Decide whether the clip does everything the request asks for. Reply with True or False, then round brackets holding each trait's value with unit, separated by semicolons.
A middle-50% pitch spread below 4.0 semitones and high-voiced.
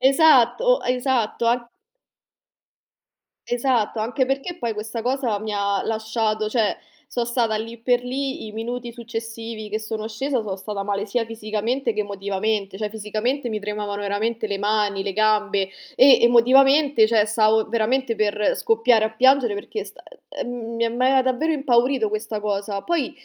True (2.8 semitones; 225 Hz)